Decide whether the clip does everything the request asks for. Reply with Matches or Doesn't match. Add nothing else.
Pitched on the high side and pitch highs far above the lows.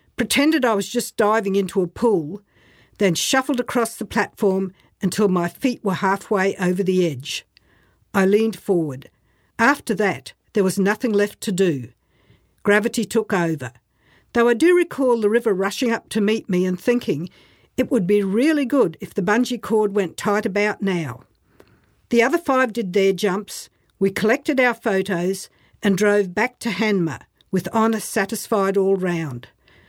Doesn't match